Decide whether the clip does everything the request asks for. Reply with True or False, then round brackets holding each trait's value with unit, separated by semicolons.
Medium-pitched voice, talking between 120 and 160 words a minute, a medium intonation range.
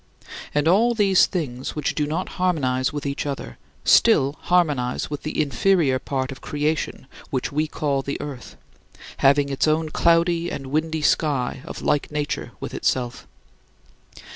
True (150 Hz; 150 wpm; 3.0 semitones)